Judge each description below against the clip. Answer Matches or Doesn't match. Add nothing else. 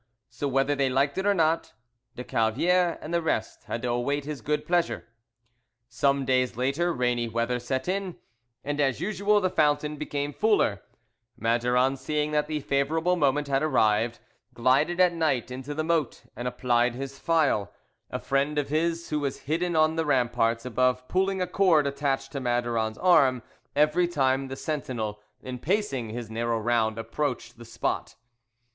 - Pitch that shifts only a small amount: Doesn't match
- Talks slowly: Doesn't match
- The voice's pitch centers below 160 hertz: Matches